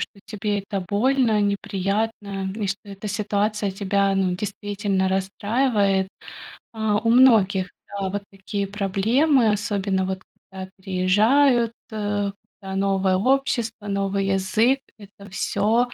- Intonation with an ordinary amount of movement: No, narrow, 2.0 semitones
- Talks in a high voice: Yes, high, 200 Hz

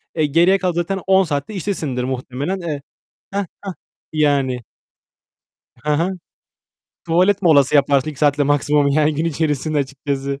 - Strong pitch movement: No, average, 3.5 semitones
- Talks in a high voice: No, medium, 150 Hz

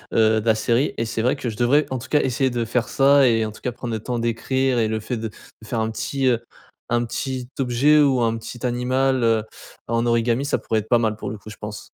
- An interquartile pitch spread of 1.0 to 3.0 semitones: Yes, narrow, 2.5 semitones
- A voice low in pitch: Yes, low, 120 Hz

